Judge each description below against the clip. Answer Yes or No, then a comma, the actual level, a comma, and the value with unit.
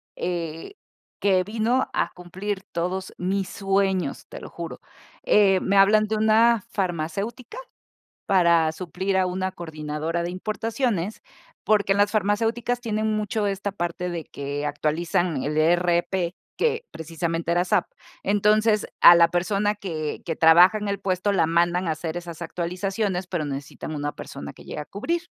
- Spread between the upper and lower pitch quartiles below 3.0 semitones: No, average, 3.5 semitones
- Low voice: No, medium, 185 Hz